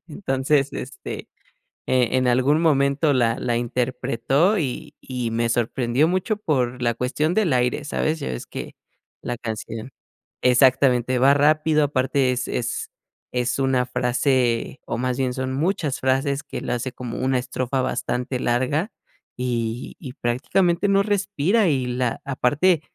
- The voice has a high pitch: No, low, 130 Hz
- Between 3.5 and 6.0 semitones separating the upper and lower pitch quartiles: No, average, 3.1 semitones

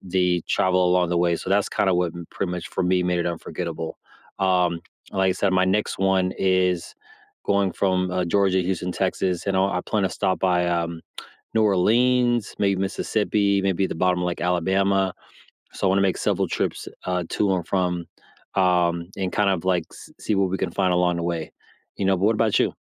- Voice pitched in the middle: No, very low, 95 Hz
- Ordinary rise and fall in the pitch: No, narrow, 1.6 semitones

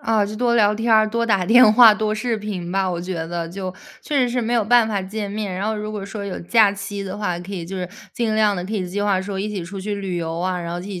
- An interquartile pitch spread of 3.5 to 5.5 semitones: No, narrow, 2.6 semitones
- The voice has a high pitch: Yes, high, 205 Hz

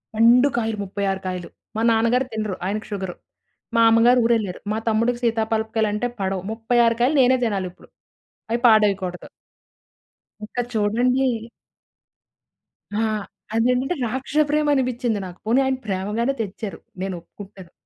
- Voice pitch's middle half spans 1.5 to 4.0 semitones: Yes, average, 3.3 semitones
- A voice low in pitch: No, high, 225 Hz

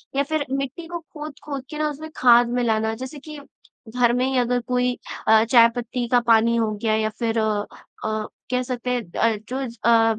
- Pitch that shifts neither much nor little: Yes, average, 3.0 semitones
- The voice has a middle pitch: No, high, 245 Hz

